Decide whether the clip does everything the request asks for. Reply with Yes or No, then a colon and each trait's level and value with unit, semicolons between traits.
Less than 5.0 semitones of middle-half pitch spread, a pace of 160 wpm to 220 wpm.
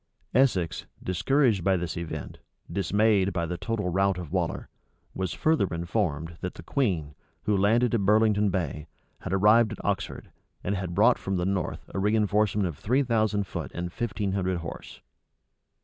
Yes: average, 3.5 semitones; average, 165 wpm